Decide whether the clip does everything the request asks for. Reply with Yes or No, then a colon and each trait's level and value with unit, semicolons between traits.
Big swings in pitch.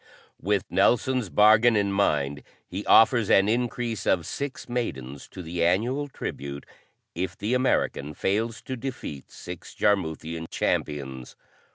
Yes: wide, 6.5 semitones